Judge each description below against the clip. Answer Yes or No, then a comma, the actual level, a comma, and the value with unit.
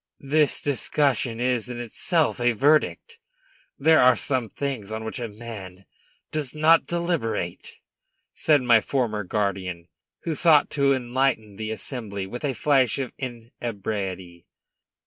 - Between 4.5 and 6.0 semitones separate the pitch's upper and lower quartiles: Yes, average, 4.8 semitones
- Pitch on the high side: No, low, 120 Hz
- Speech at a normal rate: No, slow, 130 wpm